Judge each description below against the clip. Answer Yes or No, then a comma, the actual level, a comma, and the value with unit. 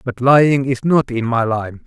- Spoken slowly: No, fast, 225 wpm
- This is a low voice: Yes, low, 125 Hz